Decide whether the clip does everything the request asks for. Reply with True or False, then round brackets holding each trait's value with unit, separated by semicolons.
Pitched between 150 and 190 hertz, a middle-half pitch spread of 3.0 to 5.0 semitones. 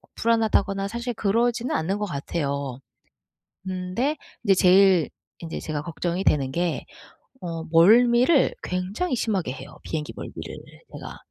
False (185 Hz; 5.5 semitones)